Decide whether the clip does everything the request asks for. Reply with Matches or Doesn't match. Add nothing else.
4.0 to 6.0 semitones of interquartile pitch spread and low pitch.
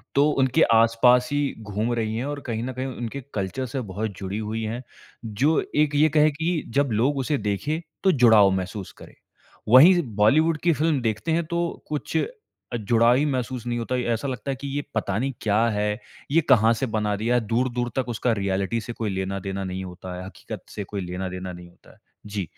Matches